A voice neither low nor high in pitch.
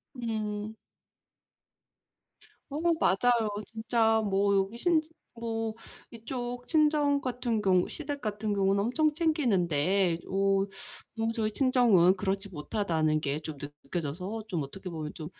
No: high, 210 Hz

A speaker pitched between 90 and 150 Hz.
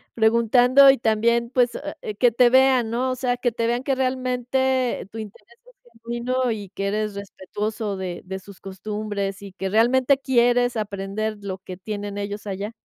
No: high, 225 Hz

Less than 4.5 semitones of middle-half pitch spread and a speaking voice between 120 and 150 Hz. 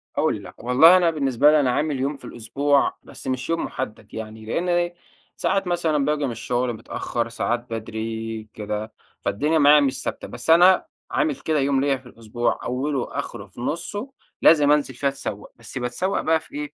No: average, 4.8 semitones; medium, 140 Hz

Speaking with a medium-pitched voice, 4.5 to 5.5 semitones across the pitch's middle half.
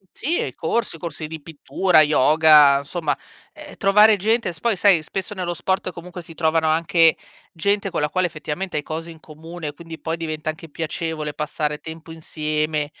No: medium, 160 Hz; narrow, 2.5 semitones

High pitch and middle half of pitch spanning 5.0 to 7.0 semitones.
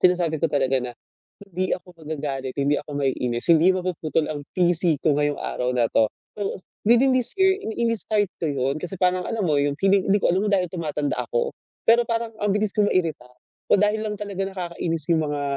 No: medium, 175 Hz; wide, 5.5 semitones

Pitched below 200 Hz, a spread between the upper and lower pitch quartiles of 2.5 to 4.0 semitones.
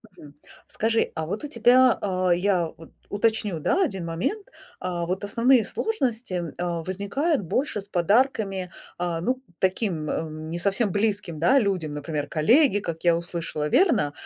No: high, 190 Hz; average, 5.2 semitones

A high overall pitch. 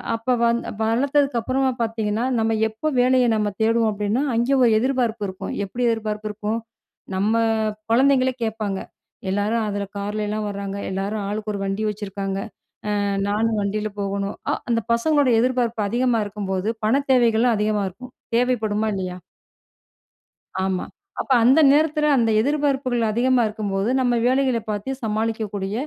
Yes: high, 225 Hz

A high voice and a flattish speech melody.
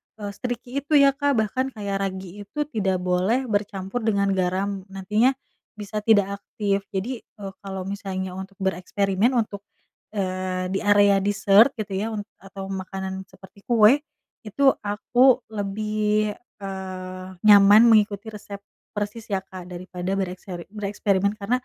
Yes: high, 200 Hz; narrow, 2.0 semitones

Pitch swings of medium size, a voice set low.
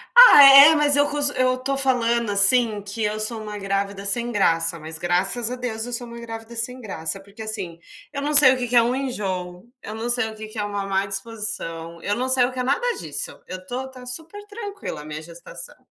No: average, 4.4 semitones; high, 230 Hz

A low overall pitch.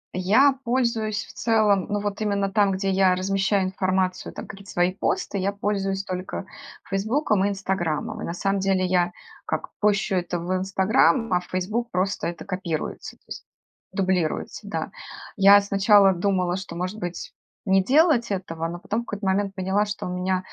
No: high, 195 Hz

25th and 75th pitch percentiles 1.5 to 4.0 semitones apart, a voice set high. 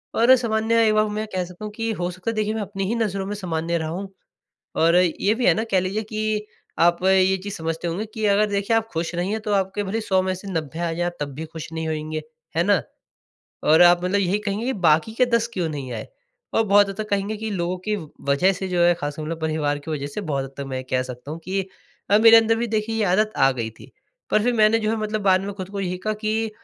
No: average, 4.5 semitones; high, 195 Hz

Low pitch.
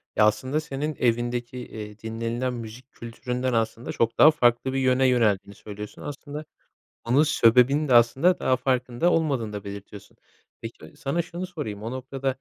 Yes: low, 125 Hz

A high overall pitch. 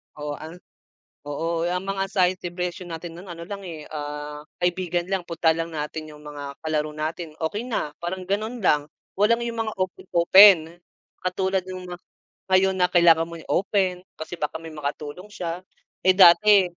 No: medium, 175 Hz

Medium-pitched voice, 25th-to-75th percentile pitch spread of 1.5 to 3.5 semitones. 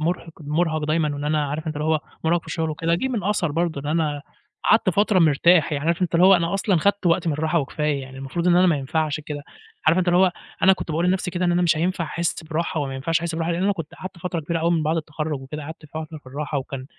Yes: medium, 160 Hz; narrow, 2.5 semitones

